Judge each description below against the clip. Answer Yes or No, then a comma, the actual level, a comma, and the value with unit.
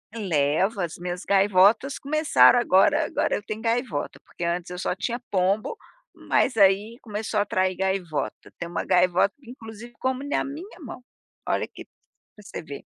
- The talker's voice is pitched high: Yes, high, 205 Hz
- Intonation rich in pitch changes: No, average, 4.7 semitones